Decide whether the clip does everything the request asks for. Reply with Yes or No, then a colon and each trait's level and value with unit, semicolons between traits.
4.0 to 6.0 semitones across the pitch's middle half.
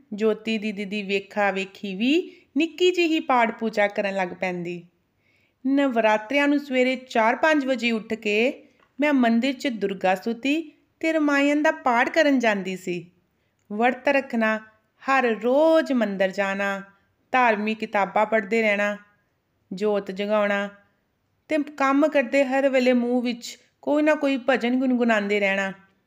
Yes: average, 5.1 semitones